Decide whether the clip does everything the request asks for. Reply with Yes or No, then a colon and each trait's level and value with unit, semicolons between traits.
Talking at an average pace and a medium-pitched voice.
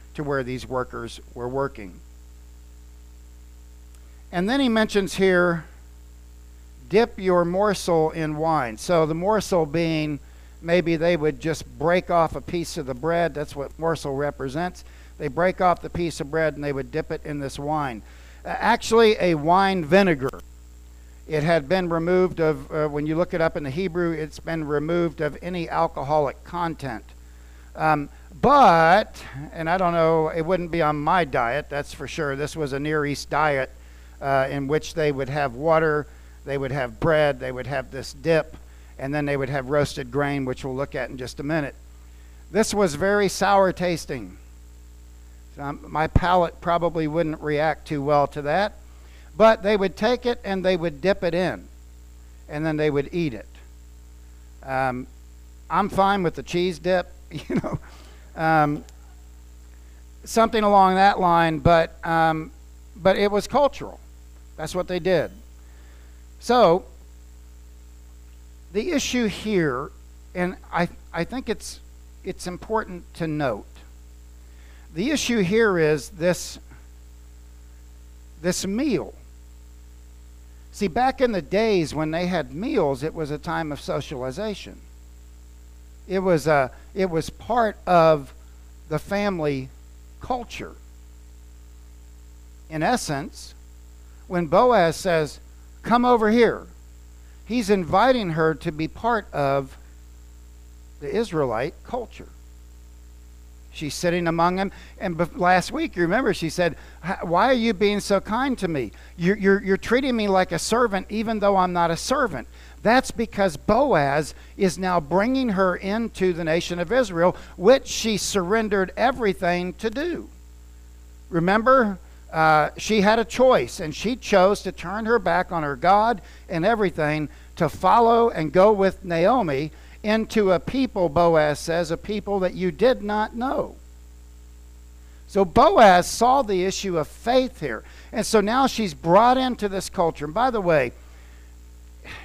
Yes: average, 150 wpm; medium, 155 Hz